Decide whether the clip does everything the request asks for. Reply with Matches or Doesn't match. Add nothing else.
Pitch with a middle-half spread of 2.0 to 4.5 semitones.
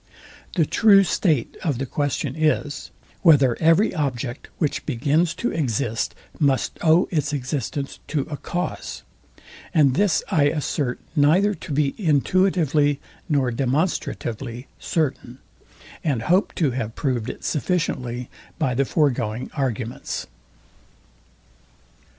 Matches